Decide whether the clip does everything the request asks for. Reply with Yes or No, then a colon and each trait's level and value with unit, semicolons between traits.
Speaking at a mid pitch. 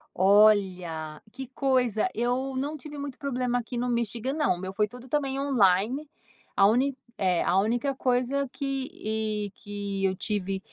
No: high, 240 Hz